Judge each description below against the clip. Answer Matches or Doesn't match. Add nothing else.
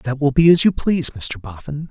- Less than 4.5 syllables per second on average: Doesn't match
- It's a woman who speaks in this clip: Doesn't match